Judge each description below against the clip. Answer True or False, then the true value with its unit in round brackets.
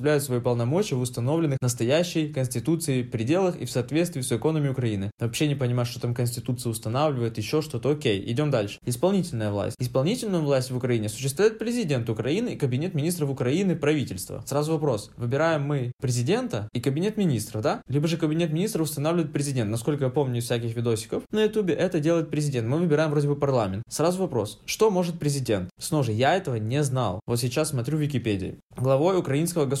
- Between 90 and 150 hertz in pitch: True (140 Hz)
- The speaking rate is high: True (180 wpm)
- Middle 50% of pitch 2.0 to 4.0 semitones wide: False (4.8 semitones)